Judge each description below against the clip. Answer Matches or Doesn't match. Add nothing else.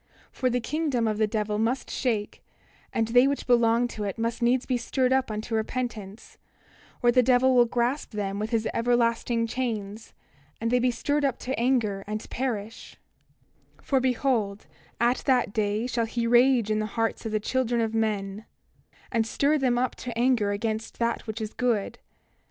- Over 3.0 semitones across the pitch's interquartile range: Doesn't match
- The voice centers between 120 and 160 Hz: Doesn't match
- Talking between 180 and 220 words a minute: Matches